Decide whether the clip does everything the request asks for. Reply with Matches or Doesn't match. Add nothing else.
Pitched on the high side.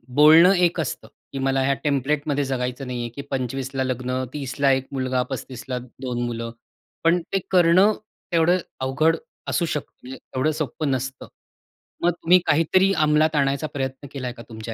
Doesn't match